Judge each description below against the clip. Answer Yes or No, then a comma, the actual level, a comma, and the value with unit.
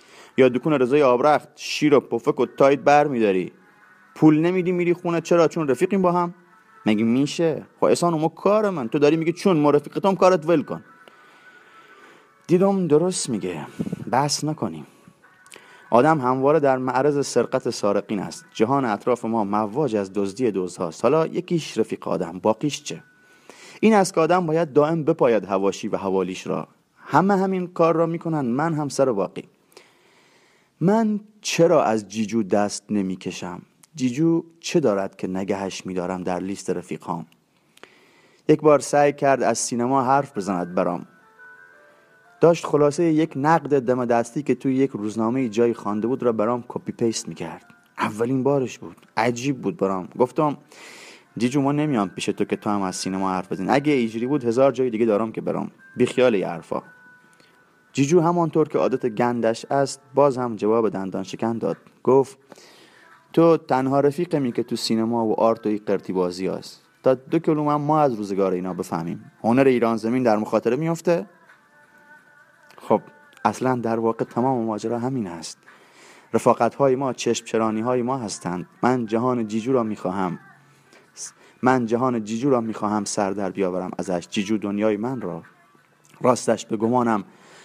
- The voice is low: Yes, low, 125 Hz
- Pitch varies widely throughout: Yes, wide, 6.5 semitones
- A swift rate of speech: Yes, fast, 160 wpm